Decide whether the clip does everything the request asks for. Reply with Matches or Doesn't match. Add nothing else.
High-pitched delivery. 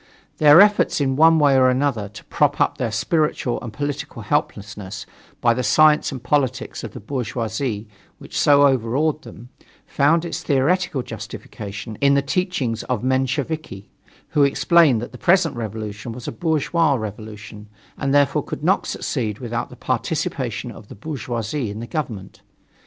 Doesn't match